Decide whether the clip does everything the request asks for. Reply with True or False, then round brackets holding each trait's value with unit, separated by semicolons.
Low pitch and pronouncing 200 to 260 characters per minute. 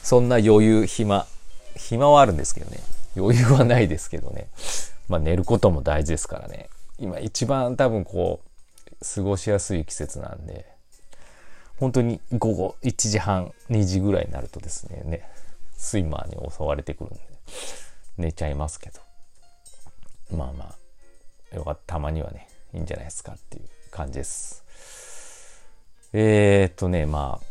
False (90 Hz; 295 characters per minute)